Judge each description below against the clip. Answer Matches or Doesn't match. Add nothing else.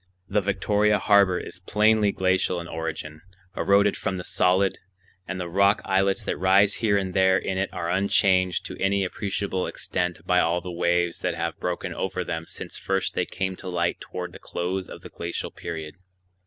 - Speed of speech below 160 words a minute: Doesn't match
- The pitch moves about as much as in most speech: Doesn't match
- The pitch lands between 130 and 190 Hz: Doesn't match